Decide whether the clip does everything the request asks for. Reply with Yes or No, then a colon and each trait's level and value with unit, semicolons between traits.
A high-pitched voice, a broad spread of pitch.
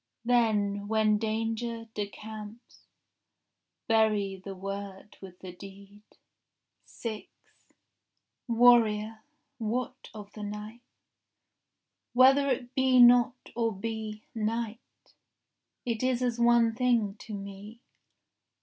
No: high, 220 Hz; narrow, 2.5 semitones